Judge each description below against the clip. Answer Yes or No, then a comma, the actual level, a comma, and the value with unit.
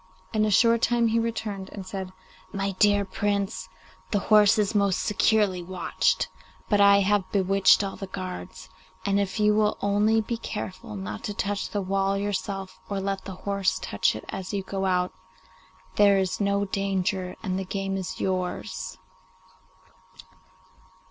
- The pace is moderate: Yes, average, 160 wpm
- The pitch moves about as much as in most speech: No, narrow, 1.5 semitones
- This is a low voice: No, high, 200 Hz